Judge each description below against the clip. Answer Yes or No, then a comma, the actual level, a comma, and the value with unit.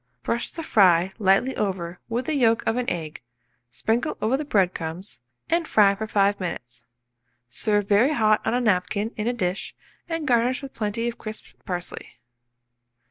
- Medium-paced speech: Yes, average, 170 wpm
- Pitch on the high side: Yes, high, 215 Hz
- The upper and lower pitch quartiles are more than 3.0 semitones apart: Yes, average, 4.6 semitones